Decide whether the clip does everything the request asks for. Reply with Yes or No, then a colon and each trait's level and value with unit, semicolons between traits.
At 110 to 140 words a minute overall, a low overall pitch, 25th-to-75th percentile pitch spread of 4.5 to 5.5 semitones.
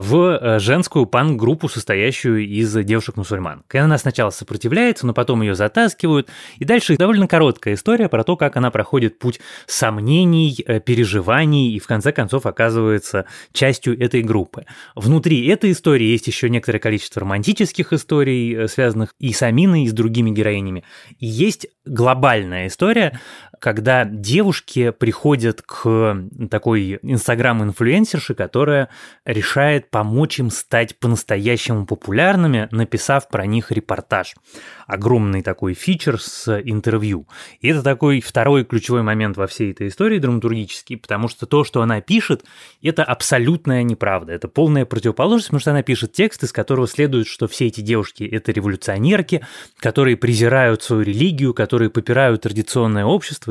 Yes: average, 135 wpm; low, 120 Hz; average, 4.8 semitones